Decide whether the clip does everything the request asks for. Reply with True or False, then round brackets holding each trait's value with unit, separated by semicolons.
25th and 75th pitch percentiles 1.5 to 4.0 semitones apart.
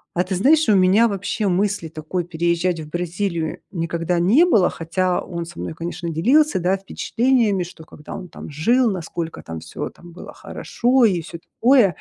True (3.7 semitones)